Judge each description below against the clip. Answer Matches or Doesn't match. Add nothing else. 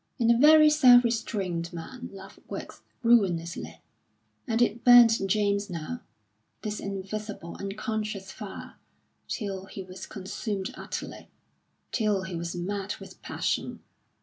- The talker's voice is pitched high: Matches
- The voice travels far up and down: Doesn't match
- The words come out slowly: Matches